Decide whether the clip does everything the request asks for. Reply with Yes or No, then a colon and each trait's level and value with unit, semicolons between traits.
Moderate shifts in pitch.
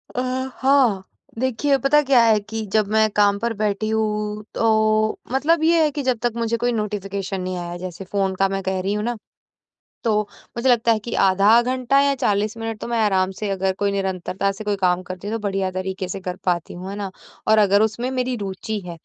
Yes: average, 3.4 semitones